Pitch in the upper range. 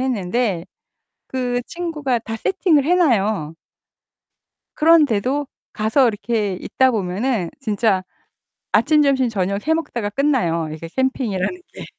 Yes: high, 240 Hz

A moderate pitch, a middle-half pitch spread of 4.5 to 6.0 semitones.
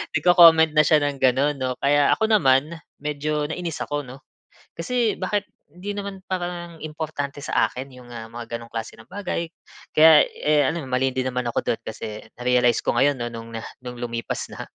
Yes: medium, 145 Hz; average, 5.0 semitones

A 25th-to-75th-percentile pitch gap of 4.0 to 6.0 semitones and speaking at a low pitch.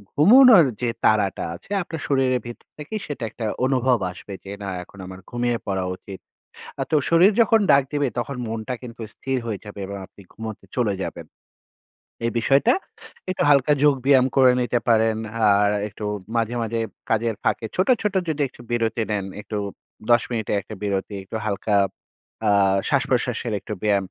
Yes: average, 4.7 semitones; low, 120 Hz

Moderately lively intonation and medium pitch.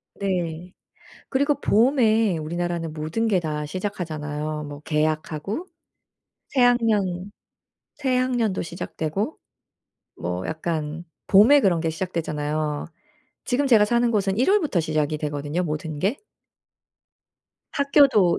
No: wide, 6.6 semitones; medium, 175 Hz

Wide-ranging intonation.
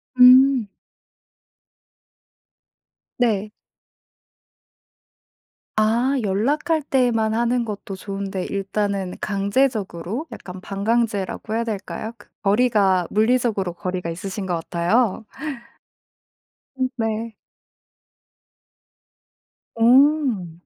No: average, 3.9 semitones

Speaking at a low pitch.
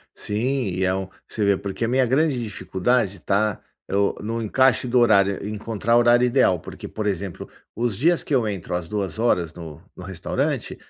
Yes: low, 105 Hz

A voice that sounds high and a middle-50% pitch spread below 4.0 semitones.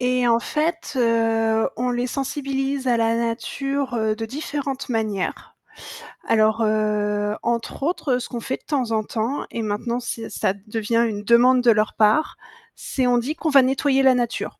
Yes: high, 235 Hz; average, 3.2 semitones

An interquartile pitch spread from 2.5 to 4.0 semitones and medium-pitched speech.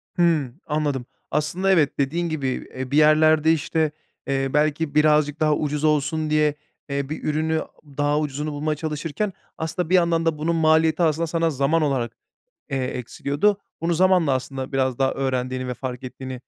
Yes: average, 2.8 semitones; medium, 150 Hz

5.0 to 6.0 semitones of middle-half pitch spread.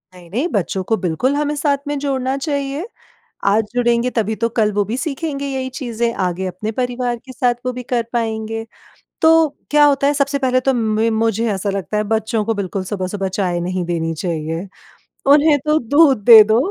Yes: wide, 5.4 semitones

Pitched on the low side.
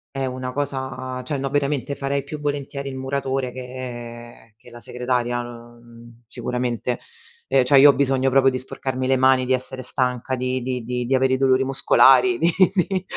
Yes: low, 130 Hz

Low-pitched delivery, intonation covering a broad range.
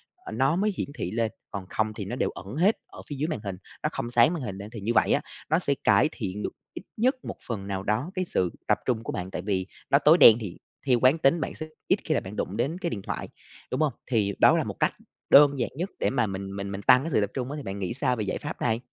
Yes: low, 120 Hz; wide, 6.8 semitones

